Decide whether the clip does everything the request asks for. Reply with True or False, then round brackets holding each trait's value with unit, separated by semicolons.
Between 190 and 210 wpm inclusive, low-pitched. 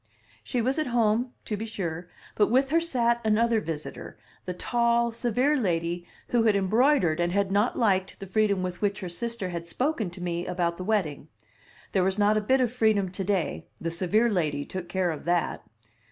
False (195 wpm; 205 Hz)